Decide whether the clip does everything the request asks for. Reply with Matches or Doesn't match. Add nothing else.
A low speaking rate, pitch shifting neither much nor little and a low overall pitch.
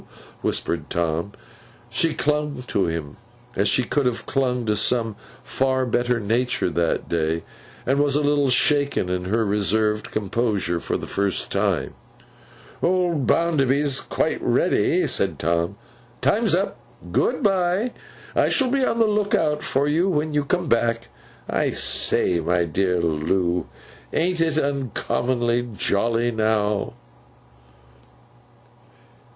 Doesn't match